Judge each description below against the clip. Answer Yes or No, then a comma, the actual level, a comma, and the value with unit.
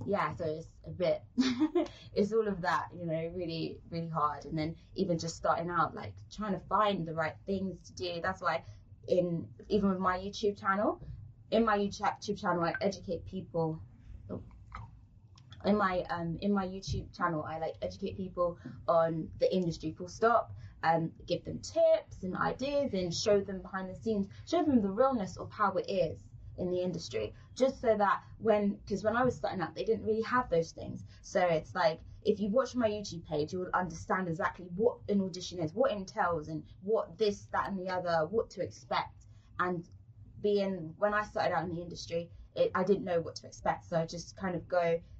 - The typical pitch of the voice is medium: Yes, medium, 180 Hz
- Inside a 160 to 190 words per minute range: No, average, 200 wpm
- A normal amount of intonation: Yes, average, 4.3 semitones